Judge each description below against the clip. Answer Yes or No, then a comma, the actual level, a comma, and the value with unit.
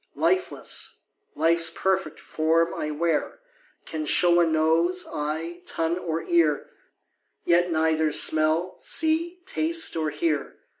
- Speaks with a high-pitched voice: No, medium, 165 Hz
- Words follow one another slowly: Yes, slow, 115 wpm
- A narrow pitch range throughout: Yes, narrow, 2.3 semitones